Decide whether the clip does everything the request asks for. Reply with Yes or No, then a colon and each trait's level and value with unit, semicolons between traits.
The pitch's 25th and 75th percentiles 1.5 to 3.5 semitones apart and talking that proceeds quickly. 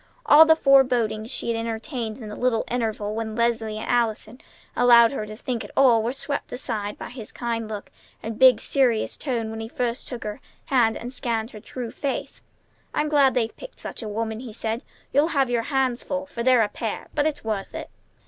Yes: average, 2.8 semitones; fast, 210 wpm